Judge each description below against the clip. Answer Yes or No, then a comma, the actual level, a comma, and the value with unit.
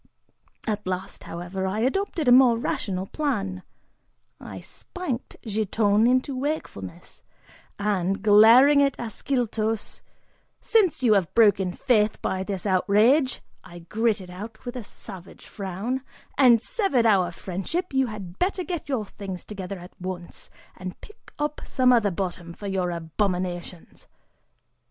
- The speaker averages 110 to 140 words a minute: Yes, slow, 135 wpm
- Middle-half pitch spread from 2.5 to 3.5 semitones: No, average, 5.3 semitones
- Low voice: No, high, 210 Hz